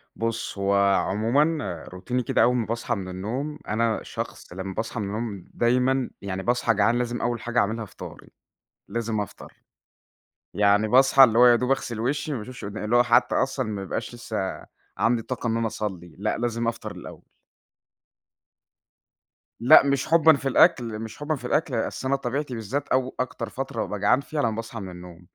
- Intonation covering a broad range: No, average, 3.2 semitones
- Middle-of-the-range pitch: No, low, 115 Hz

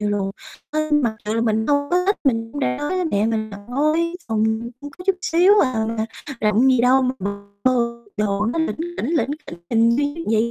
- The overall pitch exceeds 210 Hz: Yes, high, 240 Hz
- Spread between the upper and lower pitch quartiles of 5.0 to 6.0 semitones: Yes, wide, 5.5 semitones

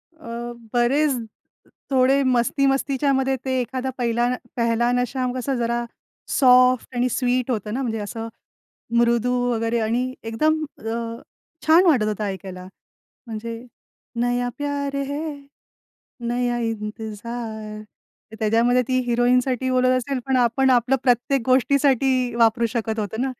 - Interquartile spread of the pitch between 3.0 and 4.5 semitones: No, narrow, 2.4 semitones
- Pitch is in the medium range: No, high, 245 Hz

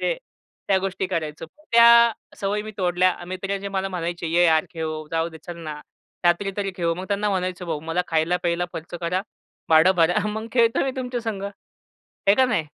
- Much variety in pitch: No, average, 3.2 semitones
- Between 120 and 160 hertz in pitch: No, medium, 180 Hz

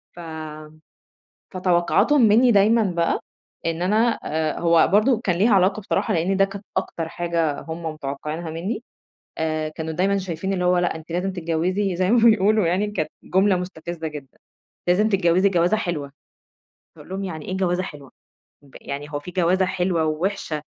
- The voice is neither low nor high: Yes, medium, 180 Hz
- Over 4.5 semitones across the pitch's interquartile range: No, average, 3.3 semitones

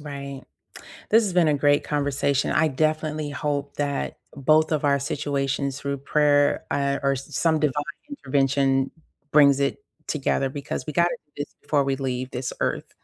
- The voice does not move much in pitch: Yes, narrow, 1.6 semitones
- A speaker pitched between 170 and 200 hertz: No, medium, 140 Hz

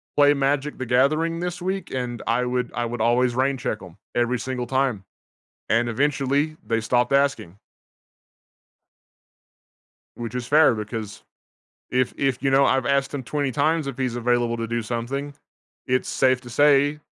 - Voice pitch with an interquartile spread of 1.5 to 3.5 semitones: Yes, average, 2.8 semitones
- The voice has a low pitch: Yes, low, 130 Hz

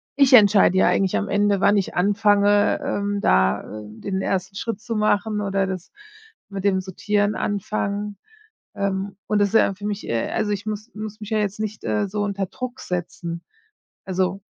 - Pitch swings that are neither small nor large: No, narrow, 1.7 semitones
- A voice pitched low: No, high, 200 Hz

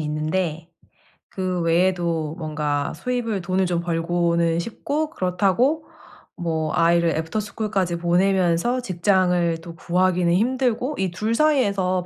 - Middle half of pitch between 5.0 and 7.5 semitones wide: No, average, 3.2 semitones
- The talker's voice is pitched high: No, medium, 180 Hz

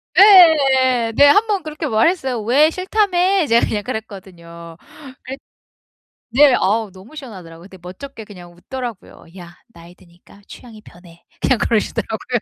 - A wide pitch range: Yes, wide, 8.0 semitones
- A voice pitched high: Yes, high, 230 Hz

